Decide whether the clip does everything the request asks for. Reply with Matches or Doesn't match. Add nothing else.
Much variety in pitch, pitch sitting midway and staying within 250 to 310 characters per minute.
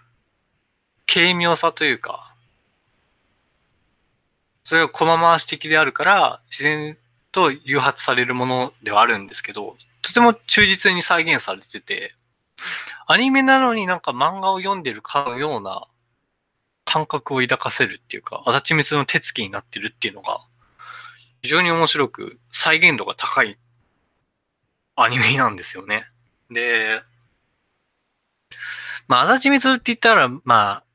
Matches